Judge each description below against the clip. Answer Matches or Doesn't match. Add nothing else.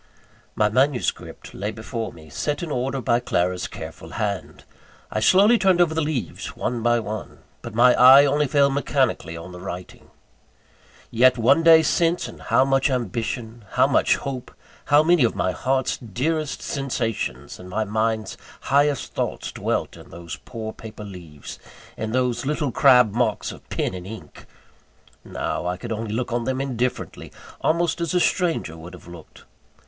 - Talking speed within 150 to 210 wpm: Matches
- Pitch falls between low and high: Doesn't match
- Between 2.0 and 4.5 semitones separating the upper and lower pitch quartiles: Doesn't match